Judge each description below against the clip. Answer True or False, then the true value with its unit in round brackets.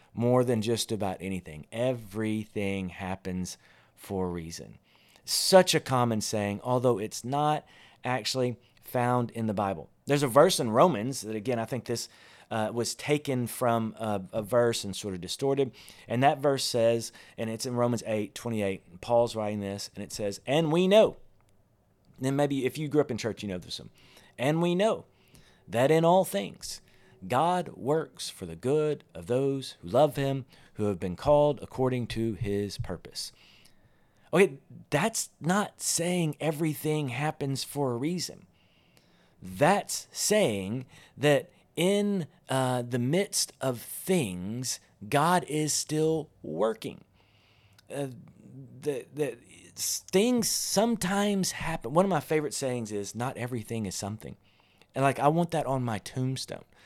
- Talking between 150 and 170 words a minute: True (155 wpm)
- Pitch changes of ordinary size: False (5.8 semitones)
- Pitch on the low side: True (125 Hz)